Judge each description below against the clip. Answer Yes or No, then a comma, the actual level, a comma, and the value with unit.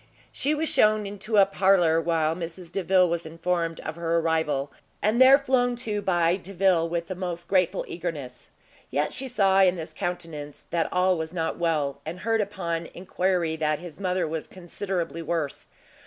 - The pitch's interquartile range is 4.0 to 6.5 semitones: No, average, 2.9 semitones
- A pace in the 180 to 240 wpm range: No, average, 170 wpm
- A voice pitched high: No, medium, 175 Hz